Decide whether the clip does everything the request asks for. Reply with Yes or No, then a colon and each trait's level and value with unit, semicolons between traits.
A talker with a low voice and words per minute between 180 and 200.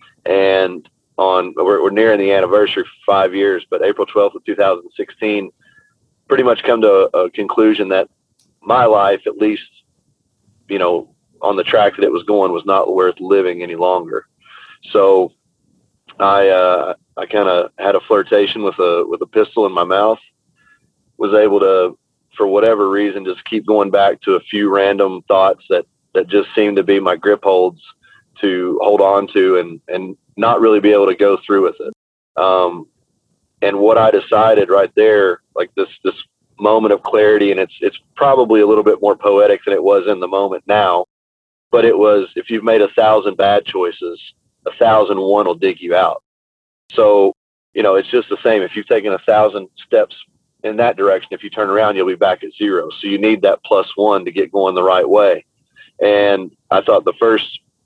Yes: low, 110 Hz; average, 195 wpm